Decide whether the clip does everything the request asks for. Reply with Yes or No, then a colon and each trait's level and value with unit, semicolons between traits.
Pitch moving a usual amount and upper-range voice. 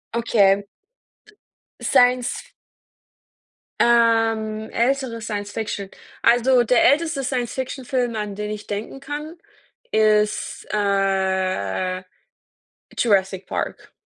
Yes: average, 3.5 semitones; high, 220 Hz